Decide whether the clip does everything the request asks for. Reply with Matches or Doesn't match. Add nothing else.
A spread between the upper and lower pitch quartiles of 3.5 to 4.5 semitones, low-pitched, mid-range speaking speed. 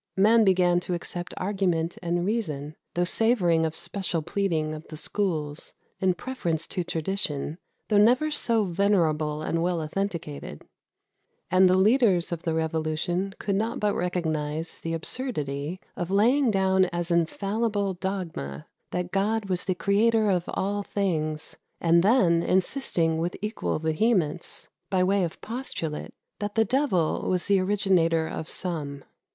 Doesn't match